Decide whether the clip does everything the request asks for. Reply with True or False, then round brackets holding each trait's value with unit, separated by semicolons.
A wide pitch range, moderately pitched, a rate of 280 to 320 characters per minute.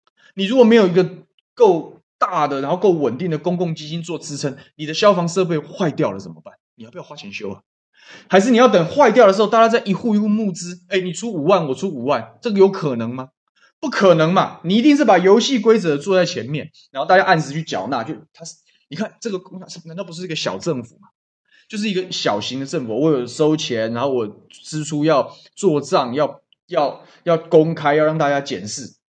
False (4.5 semitones; 175 Hz; 315 characters per minute)